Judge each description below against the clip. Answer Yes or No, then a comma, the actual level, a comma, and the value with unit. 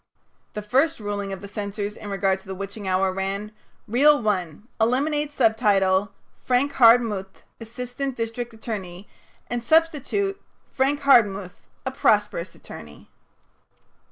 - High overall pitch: Yes, high, 215 Hz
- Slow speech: Yes, slow, 125 wpm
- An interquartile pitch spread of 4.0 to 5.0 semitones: Yes, average, 4.4 semitones